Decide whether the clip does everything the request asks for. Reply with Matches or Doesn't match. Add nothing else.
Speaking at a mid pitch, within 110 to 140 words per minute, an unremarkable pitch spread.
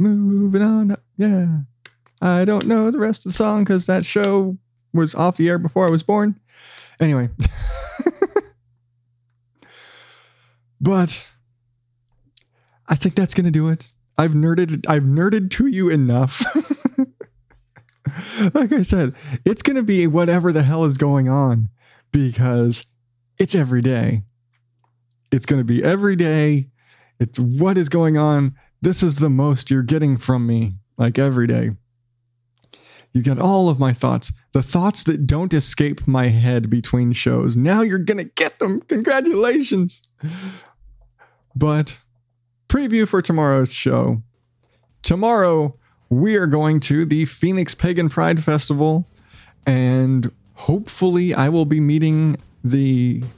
Doesn't match